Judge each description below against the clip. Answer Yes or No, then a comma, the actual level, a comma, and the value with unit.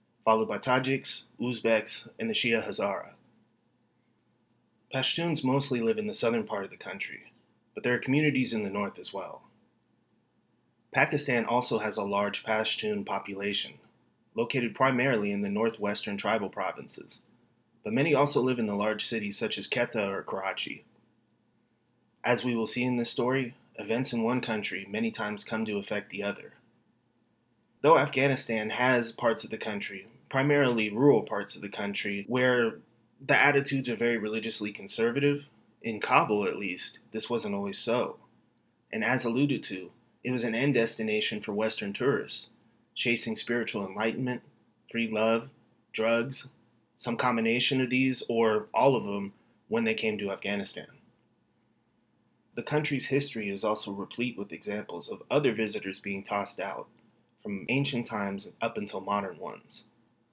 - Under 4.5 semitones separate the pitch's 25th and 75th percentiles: Yes, average, 2.8 semitones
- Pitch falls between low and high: No, low, 115 Hz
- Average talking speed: Yes, average, 150 wpm